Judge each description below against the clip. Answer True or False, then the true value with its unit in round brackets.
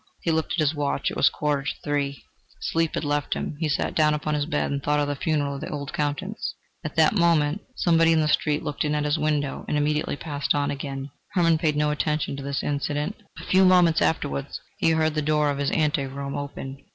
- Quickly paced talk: True (235 wpm)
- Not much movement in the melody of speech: True (1.8 semitones)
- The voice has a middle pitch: True (150 Hz)